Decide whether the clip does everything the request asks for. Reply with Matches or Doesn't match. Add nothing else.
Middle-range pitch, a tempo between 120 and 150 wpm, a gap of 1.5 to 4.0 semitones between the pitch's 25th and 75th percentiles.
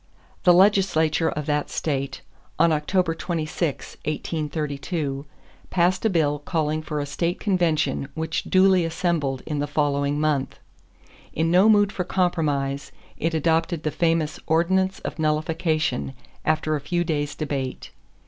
Matches